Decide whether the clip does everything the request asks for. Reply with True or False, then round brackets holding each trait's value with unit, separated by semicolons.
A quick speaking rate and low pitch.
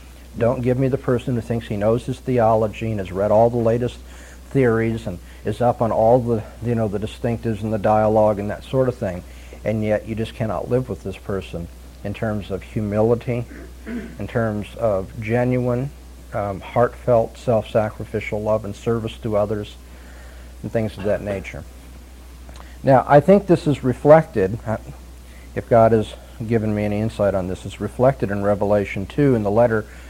False (175 wpm; 110 Hz)